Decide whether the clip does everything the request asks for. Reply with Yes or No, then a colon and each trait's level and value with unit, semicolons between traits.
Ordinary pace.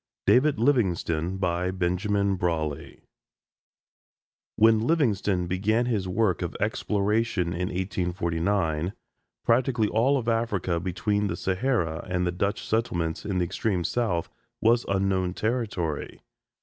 No: slow, 110 wpm